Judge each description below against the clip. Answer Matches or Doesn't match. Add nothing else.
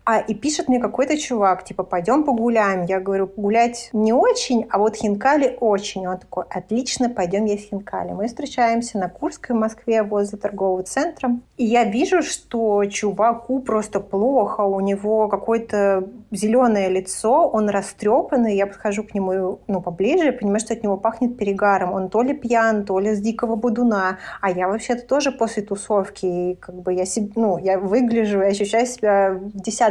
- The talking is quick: Matches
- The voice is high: Matches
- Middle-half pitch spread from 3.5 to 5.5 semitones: Doesn't match